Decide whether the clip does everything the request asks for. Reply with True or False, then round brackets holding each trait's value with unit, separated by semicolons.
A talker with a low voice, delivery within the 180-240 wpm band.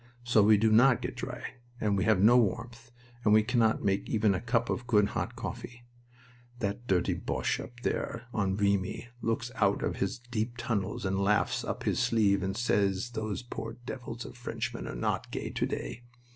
True (110 Hz; 190 wpm)